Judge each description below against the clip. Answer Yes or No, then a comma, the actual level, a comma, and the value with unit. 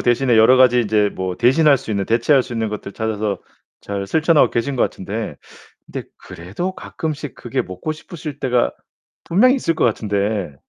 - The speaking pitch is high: No, low, 115 Hz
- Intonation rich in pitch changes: Yes, wide, 5.7 semitones